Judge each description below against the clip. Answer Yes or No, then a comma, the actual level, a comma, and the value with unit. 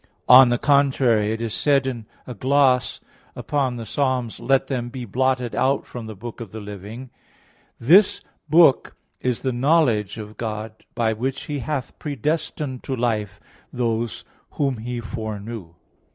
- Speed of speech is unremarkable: Yes, average, 150 wpm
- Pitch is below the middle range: Yes, low, 120 Hz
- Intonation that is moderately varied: Yes, average, 3.3 semitones